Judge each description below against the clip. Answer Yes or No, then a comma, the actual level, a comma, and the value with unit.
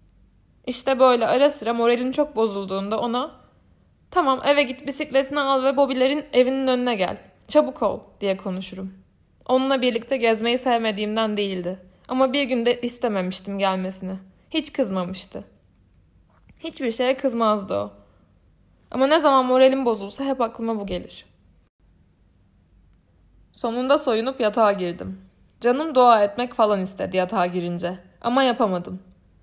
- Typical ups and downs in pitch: No, wide, 6.9 semitones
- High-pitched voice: Yes, high, 220 Hz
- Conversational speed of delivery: Yes, average, 125 wpm